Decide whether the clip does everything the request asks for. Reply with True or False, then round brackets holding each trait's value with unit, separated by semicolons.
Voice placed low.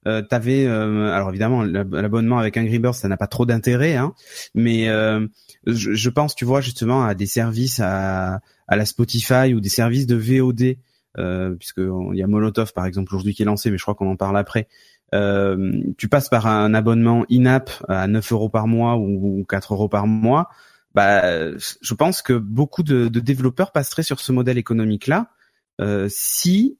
True (115 Hz)